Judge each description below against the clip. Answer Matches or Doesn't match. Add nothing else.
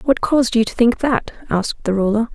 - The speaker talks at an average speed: Doesn't match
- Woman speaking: Matches